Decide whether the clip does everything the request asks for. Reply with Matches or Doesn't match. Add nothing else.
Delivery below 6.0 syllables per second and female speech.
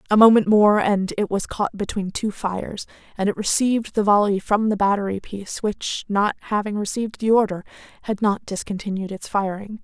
Matches